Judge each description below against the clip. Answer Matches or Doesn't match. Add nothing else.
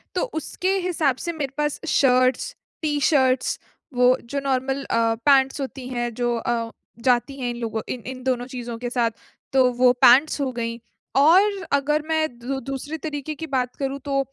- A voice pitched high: Matches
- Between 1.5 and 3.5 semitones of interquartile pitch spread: Matches